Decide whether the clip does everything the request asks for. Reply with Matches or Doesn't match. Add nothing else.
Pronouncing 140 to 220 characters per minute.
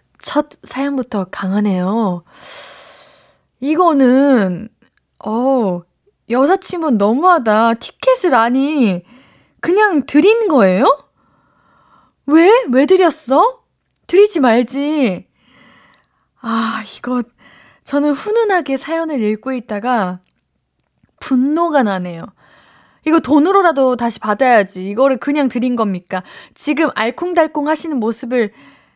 Matches